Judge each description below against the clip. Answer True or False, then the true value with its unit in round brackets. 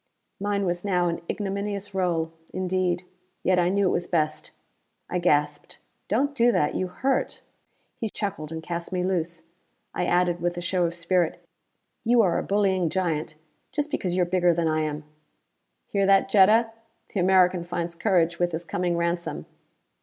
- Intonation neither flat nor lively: False (2.3 semitones)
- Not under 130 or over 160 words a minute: False (175 wpm)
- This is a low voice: False (180 Hz)